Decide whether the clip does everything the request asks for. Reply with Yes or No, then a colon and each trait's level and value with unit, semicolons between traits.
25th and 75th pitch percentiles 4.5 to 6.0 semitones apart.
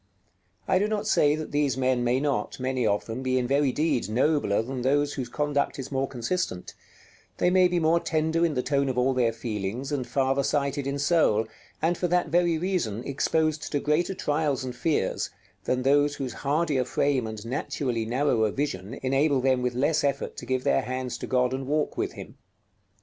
No: average, 3.1 semitones